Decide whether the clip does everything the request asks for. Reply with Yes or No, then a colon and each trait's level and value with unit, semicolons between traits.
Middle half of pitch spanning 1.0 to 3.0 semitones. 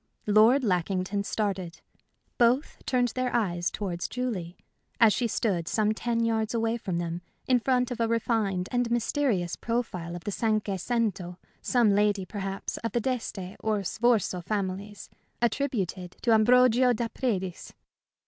No: average, 4.1 semitones